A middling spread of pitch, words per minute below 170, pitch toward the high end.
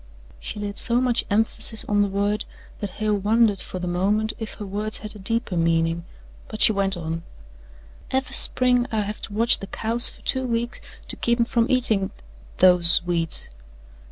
No: average, 3.2 semitones; average, 185 wpm; high, 210 Hz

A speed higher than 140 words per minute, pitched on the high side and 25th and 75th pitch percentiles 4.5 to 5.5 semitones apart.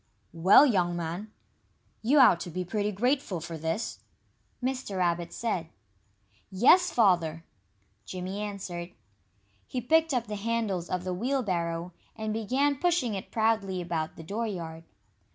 No: slow, 135 wpm; high, 195 Hz; average, 5.1 semitones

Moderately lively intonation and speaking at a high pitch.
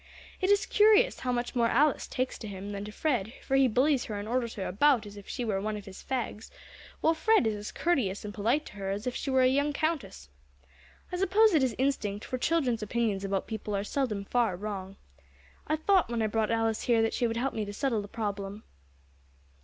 Yes: average, 4.7 semitones; high, 230 Hz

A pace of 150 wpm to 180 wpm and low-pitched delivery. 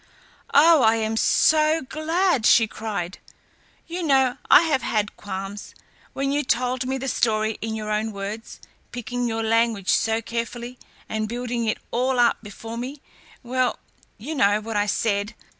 No: average, 160 wpm; high, 230 Hz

